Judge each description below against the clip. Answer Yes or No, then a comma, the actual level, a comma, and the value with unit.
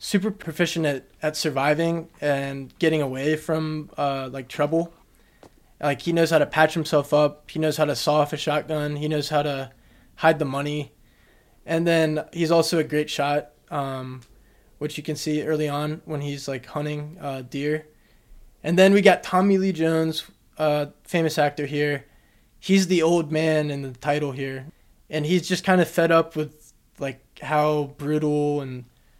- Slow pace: No, average, 175 wpm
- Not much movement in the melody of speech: Yes, narrow, 2.2 semitones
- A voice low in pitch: No, medium, 150 Hz